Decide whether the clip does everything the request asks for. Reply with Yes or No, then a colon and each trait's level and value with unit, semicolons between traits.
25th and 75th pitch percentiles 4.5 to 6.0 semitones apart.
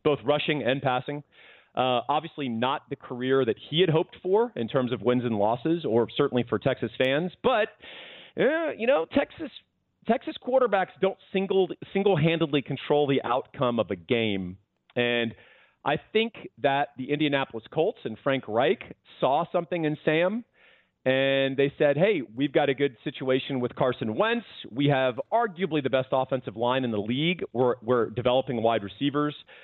Yes: average, 4.8 semitones